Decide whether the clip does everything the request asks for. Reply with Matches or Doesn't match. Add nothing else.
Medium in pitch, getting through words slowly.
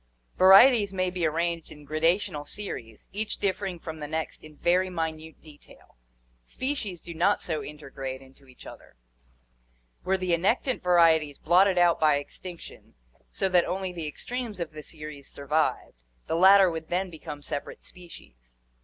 Doesn't match